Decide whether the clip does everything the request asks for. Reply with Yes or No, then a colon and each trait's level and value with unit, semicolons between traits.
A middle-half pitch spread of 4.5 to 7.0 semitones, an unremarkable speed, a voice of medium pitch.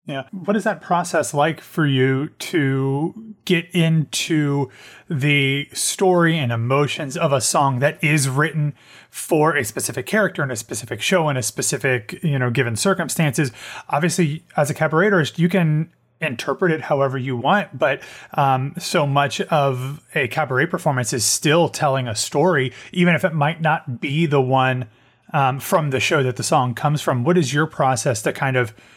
No: average, 3.8 semitones; average, 175 wpm; medium, 145 Hz